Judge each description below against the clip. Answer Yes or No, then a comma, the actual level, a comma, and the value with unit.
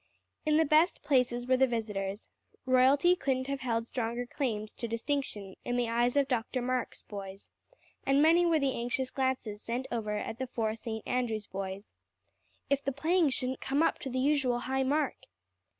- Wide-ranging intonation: No, average, 3.3 semitones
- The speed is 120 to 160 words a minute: No, average, 180 wpm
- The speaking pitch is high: Yes, very high, 255 Hz